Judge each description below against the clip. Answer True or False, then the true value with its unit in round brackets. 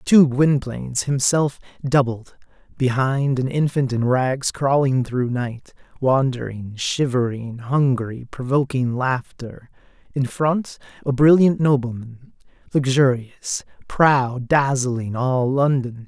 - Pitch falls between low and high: False (130 Hz)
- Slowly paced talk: True (95 wpm)